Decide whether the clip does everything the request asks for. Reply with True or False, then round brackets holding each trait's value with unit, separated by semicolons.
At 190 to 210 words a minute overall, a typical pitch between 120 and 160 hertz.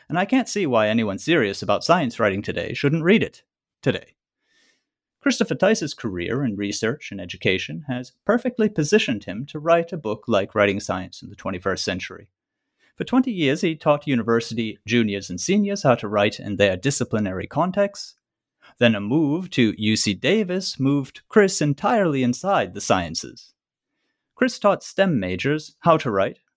False (165 wpm; 140 Hz)